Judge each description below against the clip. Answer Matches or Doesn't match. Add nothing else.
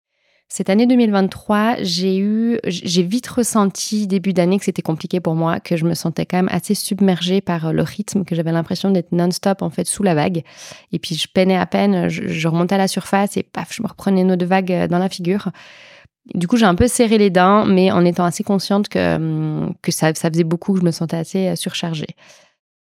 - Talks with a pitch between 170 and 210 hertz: Matches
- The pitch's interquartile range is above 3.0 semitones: Doesn't match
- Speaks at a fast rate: Matches